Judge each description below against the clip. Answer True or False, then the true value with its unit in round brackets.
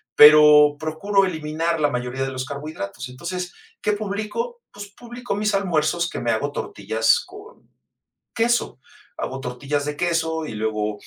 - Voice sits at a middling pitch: True (155 Hz)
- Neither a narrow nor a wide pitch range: False (7.0 semitones)